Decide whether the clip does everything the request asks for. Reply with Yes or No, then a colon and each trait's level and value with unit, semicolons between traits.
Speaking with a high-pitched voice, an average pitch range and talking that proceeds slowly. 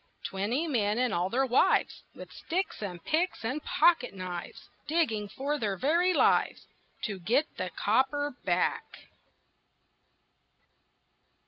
No: very high, 250 Hz; wide, 6.8 semitones; slow, 120 wpm